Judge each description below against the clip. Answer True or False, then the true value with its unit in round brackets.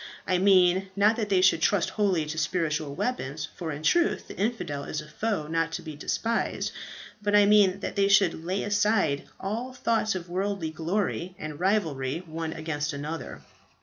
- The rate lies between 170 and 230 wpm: True (180 wpm)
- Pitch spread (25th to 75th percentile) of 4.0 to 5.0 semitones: True (4.6 semitones)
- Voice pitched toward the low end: False (180 Hz)